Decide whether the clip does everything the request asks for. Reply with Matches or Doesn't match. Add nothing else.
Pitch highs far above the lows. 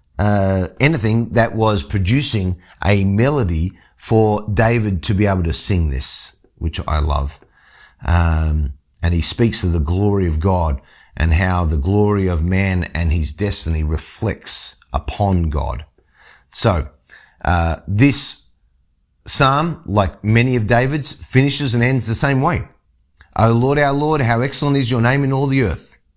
Matches